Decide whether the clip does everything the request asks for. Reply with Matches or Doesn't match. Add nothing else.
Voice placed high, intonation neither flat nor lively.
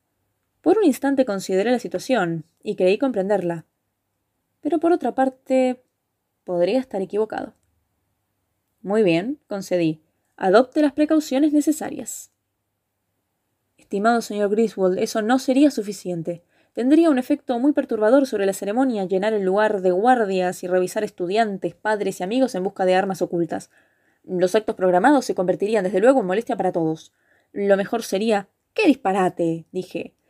Doesn't match